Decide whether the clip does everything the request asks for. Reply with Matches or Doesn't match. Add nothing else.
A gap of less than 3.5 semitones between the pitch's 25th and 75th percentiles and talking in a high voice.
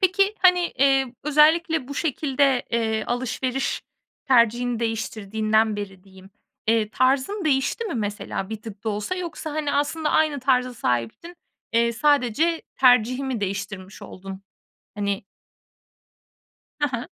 Doesn't match